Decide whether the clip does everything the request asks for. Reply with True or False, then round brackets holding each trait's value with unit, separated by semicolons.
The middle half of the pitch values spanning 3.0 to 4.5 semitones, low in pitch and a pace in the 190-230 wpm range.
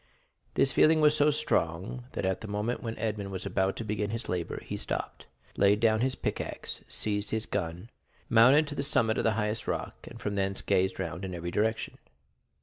True (3.4 semitones; 105 Hz; 200 wpm)